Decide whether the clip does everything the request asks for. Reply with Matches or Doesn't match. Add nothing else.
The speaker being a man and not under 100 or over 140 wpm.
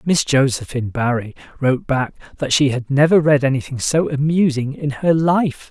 Doesn't match